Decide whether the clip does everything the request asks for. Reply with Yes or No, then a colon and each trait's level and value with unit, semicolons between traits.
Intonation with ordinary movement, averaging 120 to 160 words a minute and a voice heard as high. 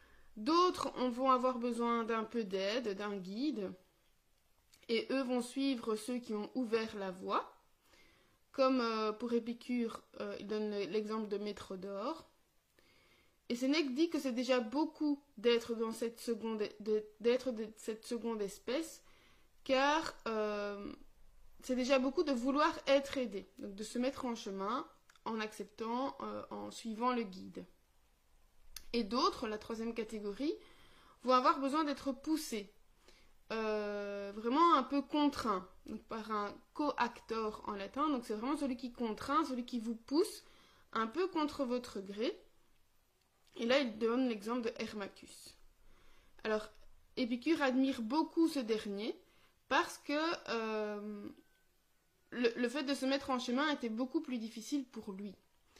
Yes: average, 4.1 semitones; slow, 145 wpm; high, 235 Hz